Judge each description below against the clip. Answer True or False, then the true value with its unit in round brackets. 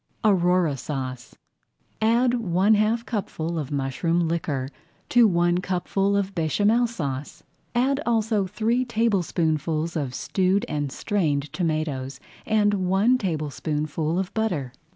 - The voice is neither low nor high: True (180 Hz)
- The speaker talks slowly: True (115 wpm)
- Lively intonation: True (5.8 semitones)